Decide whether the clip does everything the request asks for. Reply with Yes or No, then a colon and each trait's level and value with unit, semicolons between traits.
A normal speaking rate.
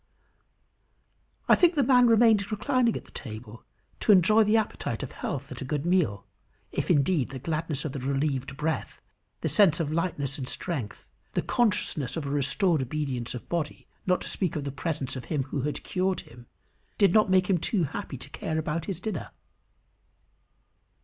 Yes: average, 185 wpm